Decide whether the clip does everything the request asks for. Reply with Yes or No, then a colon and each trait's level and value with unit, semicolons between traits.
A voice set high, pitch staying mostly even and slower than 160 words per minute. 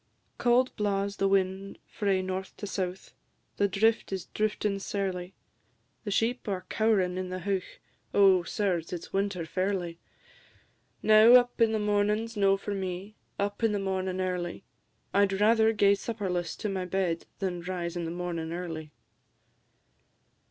Yes: high, 195 Hz; narrow, 2.2 semitones; average, 150 wpm